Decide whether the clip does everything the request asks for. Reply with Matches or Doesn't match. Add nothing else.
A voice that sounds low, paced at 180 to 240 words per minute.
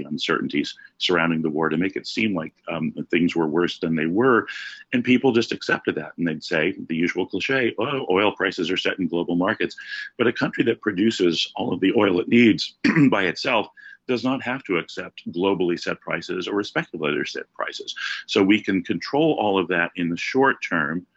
Matches